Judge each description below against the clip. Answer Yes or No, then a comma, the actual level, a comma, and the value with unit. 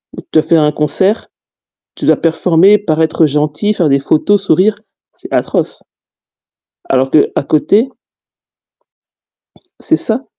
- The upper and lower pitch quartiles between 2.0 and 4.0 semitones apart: No, average, 5.2 semitones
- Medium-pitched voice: Yes, medium, 165 Hz